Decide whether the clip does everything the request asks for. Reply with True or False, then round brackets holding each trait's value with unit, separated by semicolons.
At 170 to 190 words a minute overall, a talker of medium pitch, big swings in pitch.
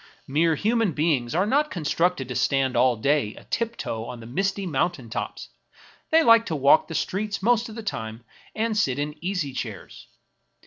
True (180 wpm; 160 Hz; 8.3 semitones)